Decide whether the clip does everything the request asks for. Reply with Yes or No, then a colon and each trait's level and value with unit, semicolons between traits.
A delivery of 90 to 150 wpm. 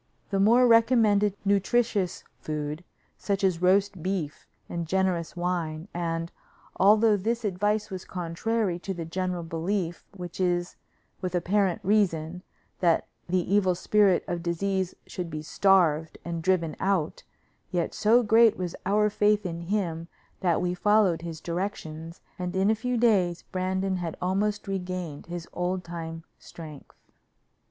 Yes: average, 140 wpm